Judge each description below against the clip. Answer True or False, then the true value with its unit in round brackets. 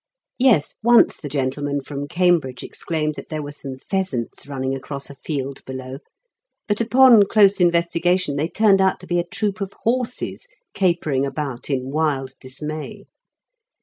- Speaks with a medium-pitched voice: True (155 Hz)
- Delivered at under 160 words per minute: True (150 wpm)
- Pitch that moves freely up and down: True (5.7 semitones)